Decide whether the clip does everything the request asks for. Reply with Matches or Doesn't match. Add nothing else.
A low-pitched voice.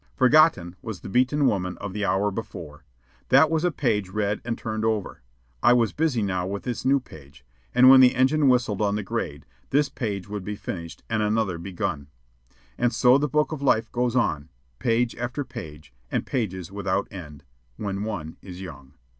Matches